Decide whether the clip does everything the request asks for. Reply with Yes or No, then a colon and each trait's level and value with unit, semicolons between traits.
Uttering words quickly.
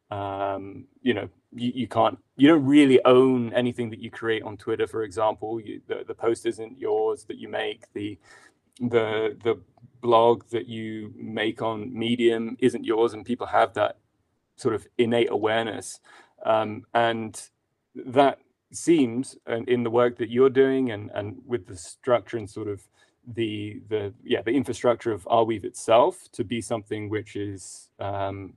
No: average, 170 wpm